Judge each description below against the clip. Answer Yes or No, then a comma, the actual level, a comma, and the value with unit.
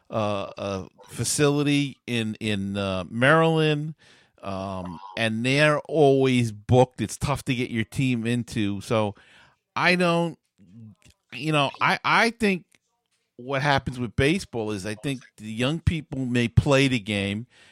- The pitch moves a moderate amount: Yes, average, 4.9 semitones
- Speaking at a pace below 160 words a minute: Yes, average, 140 wpm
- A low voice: Yes, low, 125 Hz